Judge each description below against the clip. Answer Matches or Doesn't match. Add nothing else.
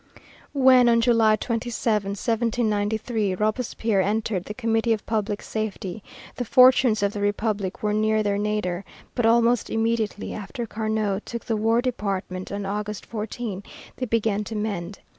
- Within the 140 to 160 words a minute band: Matches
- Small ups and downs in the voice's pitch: Matches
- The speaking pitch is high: Matches